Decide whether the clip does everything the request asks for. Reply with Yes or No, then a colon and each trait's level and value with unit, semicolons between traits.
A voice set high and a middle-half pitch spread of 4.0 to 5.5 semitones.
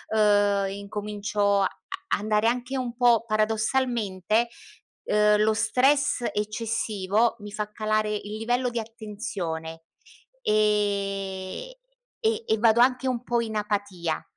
No: high, 215 Hz; narrow, 2.5 semitones